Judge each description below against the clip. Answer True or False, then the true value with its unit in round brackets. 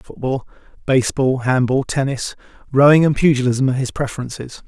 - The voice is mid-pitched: False (130 Hz)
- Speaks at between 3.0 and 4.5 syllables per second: False (5.8 syllables/s)